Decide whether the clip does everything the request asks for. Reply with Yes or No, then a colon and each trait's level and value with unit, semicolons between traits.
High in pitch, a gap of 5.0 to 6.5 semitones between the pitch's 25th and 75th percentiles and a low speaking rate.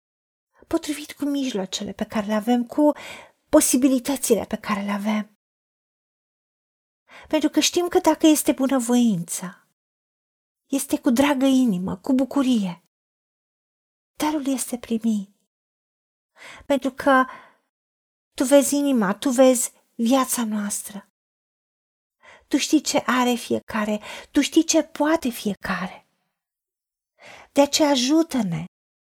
Yes: very high, 265 Hz; wide, 5.4 semitones; slow, 105 wpm